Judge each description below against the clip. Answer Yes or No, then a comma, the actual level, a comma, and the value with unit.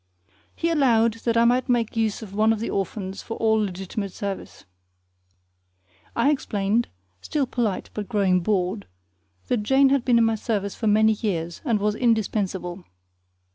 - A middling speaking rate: Yes, average, 160 wpm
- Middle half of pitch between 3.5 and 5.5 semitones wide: No, average, 2.9 semitones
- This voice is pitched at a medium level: No, high, 220 Hz